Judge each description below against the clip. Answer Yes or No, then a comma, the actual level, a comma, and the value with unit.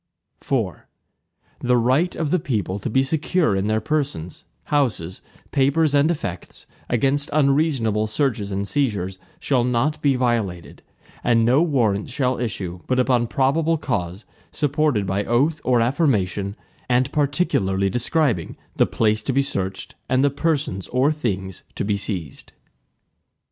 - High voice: No, low, 125 Hz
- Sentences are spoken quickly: No, average, 140 wpm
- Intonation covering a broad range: Yes, wide, 6.0 semitones